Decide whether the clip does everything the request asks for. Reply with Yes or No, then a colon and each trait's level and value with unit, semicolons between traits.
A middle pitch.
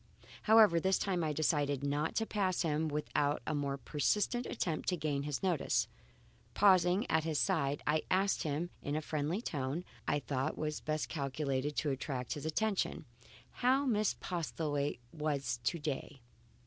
Yes: medium, 155 Hz